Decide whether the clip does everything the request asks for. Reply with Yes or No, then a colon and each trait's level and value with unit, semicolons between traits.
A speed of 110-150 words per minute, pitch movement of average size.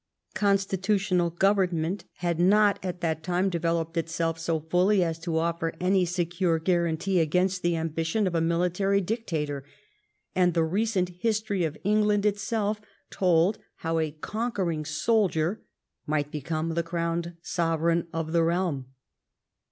Yes: slow, 135 wpm; average, 3.0 semitones